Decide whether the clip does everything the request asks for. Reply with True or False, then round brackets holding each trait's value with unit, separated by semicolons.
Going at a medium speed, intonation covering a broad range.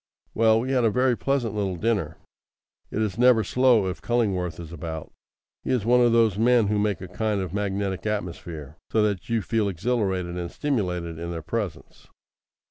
False (185 wpm; 4.4 semitones)